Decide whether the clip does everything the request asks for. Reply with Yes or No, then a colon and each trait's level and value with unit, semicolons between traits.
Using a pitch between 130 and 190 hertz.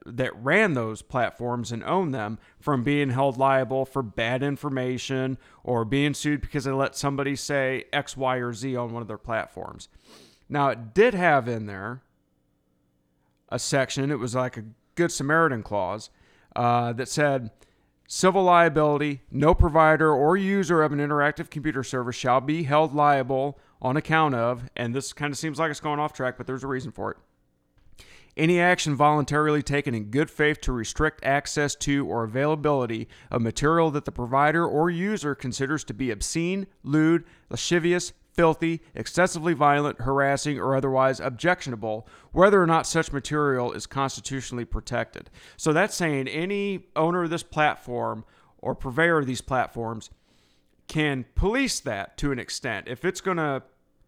Yes: medium, 140 Hz